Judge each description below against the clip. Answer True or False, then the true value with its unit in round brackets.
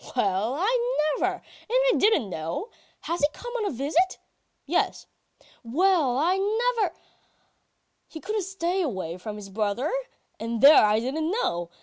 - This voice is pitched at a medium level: False (310 Hz)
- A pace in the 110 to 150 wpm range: True (145 wpm)